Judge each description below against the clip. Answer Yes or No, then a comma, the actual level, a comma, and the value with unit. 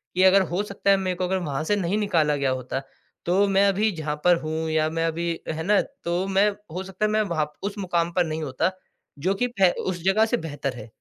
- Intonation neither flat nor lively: Yes, average, 3.7 semitones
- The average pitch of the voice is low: No, medium, 180 Hz